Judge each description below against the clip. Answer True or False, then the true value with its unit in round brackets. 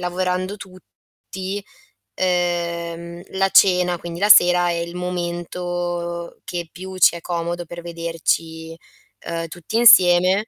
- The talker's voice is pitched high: False (175 Hz)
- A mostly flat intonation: True (1.2 semitones)